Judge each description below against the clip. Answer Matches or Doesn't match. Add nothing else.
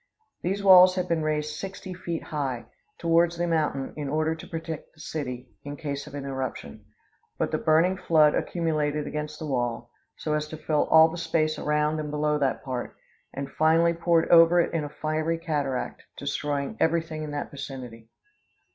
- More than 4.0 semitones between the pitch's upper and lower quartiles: Doesn't match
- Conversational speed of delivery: Matches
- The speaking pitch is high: Doesn't match